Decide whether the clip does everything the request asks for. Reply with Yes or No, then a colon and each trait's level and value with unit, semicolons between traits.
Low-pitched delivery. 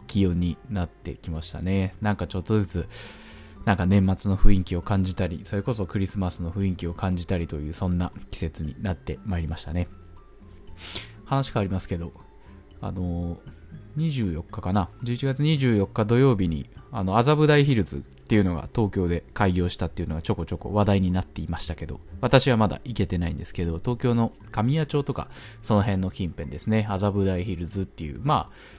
Yes: very low, 95 Hz